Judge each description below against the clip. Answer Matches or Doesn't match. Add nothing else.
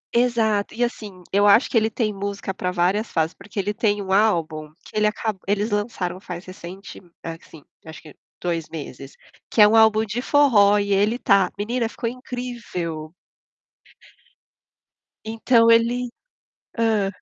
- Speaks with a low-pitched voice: Doesn't match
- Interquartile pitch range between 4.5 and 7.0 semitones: Doesn't match